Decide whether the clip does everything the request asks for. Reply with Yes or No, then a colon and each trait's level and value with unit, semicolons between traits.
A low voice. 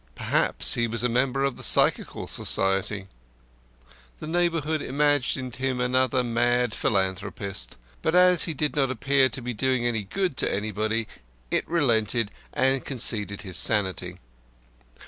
Yes: low, 125 Hz